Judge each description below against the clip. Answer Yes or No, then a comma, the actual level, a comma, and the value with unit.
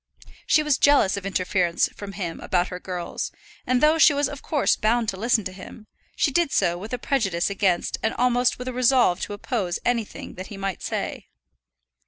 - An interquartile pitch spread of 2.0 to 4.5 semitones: No, average, 5.3 semitones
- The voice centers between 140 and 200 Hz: No, high, 215 Hz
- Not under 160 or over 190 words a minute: No, average, 200 wpm